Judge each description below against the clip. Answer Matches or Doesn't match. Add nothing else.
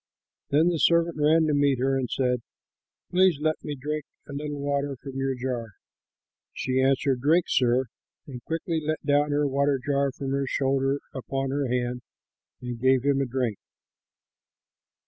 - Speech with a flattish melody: Matches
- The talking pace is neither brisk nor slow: Matches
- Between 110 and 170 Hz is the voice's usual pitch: Matches